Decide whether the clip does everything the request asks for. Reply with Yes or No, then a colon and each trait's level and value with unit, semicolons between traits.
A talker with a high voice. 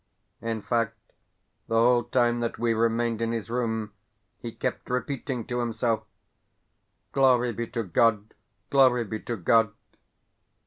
No: low, 115 Hz